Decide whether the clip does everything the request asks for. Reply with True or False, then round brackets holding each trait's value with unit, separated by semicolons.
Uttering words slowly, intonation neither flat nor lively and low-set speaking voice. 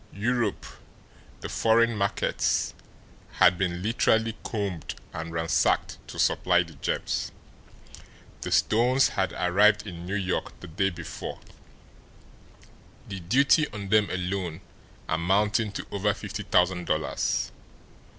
True (115 wpm; 3.4 semitones; 95 Hz)